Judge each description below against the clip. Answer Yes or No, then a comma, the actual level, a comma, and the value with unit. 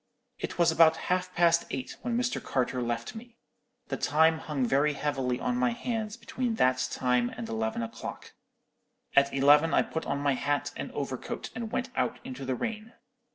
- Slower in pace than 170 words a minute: No, average, 180 wpm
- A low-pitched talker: No, medium, 145 Hz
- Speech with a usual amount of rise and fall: No, wide, 6.3 semitones